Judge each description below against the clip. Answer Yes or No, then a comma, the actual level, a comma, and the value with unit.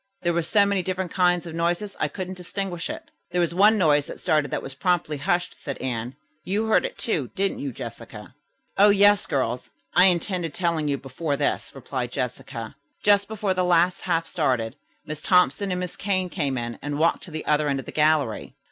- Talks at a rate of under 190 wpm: No, fast, 205 wpm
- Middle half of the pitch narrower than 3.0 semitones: No, average, 4.6 semitones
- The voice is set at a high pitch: No, medium, 170 Hz